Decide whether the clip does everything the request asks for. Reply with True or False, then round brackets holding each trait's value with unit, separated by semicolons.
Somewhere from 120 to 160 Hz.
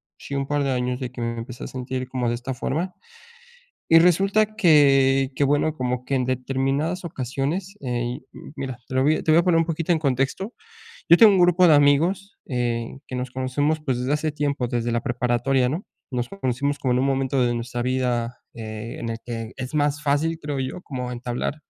True (135 Hz)